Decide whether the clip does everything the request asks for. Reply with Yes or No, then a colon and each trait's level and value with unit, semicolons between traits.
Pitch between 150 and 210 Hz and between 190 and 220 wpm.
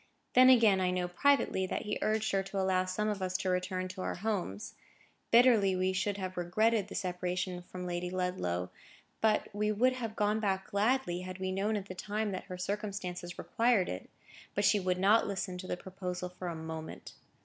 Yes: high, 190 Hz; average, 200 wpm